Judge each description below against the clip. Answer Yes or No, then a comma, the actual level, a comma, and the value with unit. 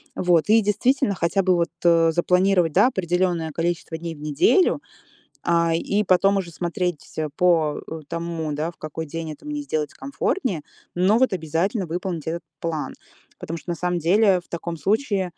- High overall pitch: No, medium, 175 Hz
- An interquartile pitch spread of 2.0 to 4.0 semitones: Yes, average, 2.8 semitones